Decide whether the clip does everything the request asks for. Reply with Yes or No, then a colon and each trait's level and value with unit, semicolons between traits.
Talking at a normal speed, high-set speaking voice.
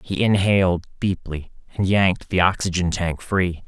No: average, 145 wpm; very low, 95 Hz